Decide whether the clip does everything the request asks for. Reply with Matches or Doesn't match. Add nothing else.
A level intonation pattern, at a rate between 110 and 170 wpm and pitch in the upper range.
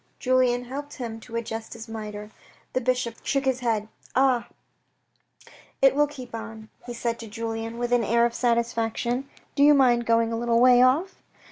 Doesn't match